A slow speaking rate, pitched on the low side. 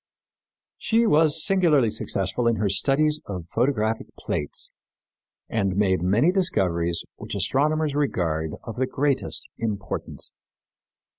Yes: slow, 115 wpm; low, 115 Hz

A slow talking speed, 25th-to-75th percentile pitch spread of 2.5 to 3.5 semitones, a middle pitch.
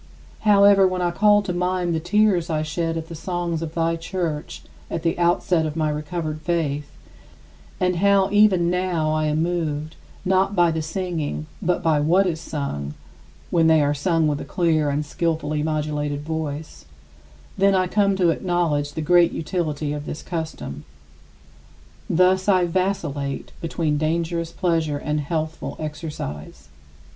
No: average, 155 wpm; average, 2.8 semitones; medium, 165 Hz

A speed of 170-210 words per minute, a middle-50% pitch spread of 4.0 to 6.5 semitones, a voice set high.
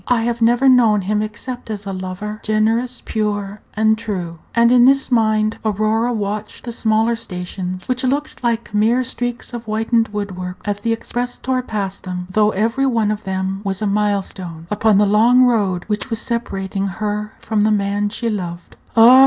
No: average, 185 wpm; average, 2.7 semitones; high, 215 Hz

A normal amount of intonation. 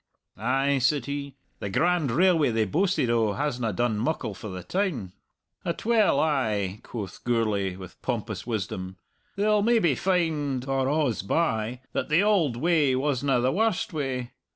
No: wide, 6.4 semitones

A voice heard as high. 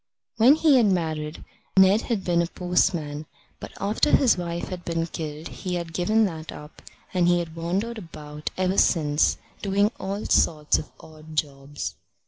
No: medium, 170 Hz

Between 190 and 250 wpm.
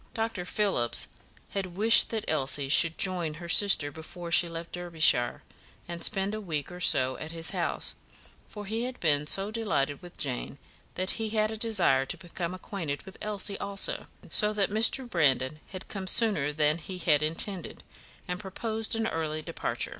No: average, 175 wpm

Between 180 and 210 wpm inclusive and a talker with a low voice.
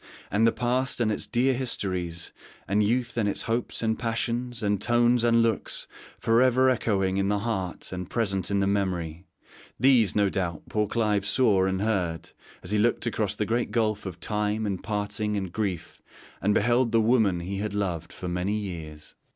Yes: average, 185 wpm; low, 105 Hz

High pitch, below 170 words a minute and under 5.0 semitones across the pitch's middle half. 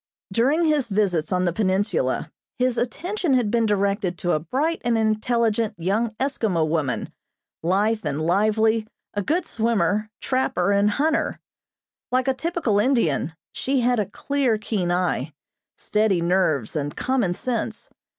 No: high, 215 Hz; average, 140 wpm; wide, 5.5 semitones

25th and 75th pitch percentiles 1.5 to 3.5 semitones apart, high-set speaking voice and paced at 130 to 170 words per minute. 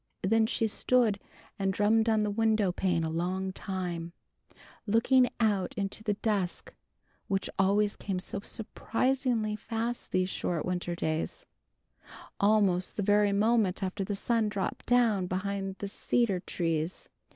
Yes: average, 3.0 semitones; high, 200 Hz; average, 140 wpm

